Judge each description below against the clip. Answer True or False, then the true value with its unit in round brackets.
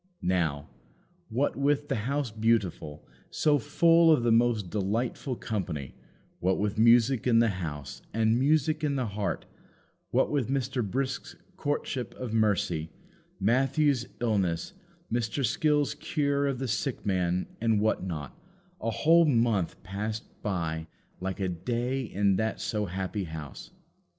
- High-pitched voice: False (115 Hz)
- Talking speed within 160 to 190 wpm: False (140 wpm)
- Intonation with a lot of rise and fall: True (5.7 semitones)